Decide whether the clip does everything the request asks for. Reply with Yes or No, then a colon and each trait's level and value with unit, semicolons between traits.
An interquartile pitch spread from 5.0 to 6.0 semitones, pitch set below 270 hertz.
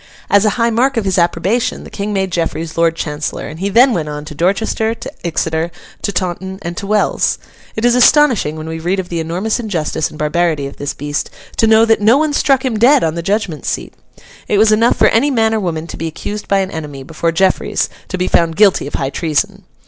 Yes: average, 5.3 semitones; high, 190 Hz